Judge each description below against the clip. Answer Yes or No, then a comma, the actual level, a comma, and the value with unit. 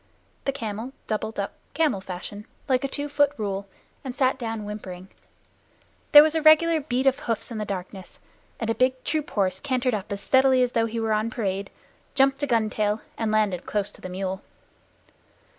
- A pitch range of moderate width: Yes, average, 4.7 semitones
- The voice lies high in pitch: Yes, high, 225 Hz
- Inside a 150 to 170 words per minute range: No, average, 190 wpm